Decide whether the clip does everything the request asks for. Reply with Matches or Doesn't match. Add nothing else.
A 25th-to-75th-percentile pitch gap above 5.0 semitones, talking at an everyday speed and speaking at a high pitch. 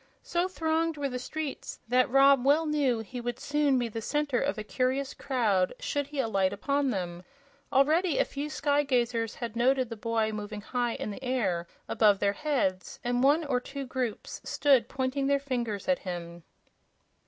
Doesn't match